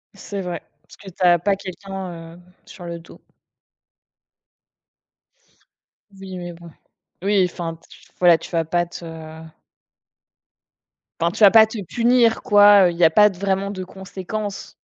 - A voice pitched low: No, high, 190 Hz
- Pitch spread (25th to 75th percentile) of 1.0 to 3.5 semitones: Yes, average, 2.7 semitones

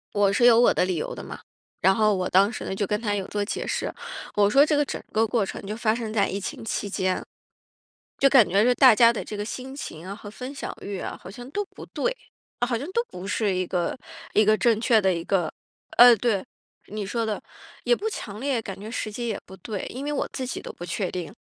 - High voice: Yes, high, 215 Hz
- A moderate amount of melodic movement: Yes, average, 3.8 semitones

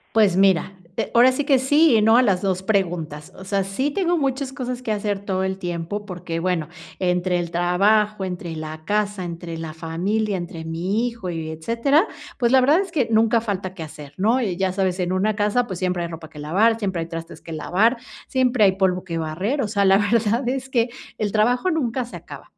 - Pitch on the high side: Yes, high, 195 Hz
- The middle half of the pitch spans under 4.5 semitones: No, average, 4.9 semitones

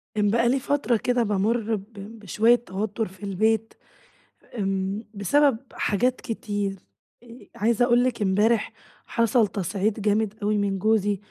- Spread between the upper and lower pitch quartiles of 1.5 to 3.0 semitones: Yes, narrow, 2.6 semitones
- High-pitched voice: Yes, high, 215 Hz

